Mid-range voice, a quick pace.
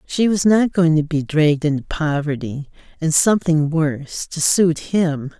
No: medium, 160 Hz; average, 165 wpm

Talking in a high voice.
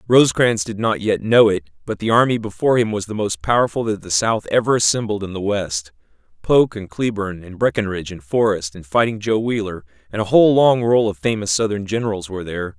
No: low, 105 Hz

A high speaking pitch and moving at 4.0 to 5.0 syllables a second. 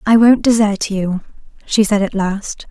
Yes: high, 210 Hz; 4.2 syllables/s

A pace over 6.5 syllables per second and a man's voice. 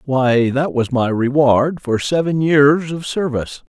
No: 3.9 syllables/s; male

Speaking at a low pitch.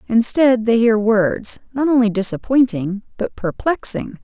No: high, 225 Hz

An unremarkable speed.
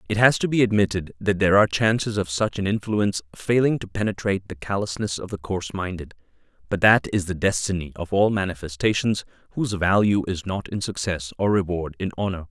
Yes: average, 190 wpm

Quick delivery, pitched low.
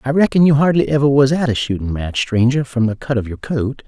Yes: fast, 265 wpm; low, 130 Hz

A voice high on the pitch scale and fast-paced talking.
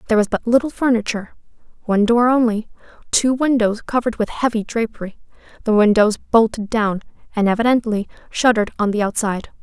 No: high, 225 Hz; average, 150 wpm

